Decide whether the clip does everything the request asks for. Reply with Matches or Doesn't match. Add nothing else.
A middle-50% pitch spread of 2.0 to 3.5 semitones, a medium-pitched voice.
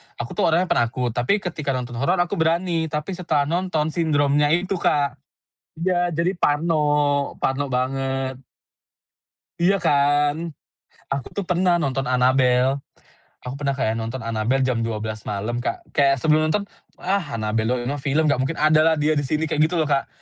Doesn't match